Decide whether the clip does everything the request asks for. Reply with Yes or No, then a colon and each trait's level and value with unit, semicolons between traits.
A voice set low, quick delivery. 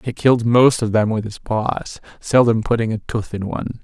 Yes: low, 115 Hz; fast, 220 wpm